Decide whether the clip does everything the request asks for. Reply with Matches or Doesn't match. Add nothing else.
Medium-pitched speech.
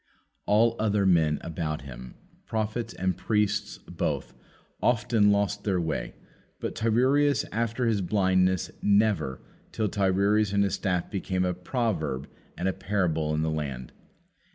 Doesn't match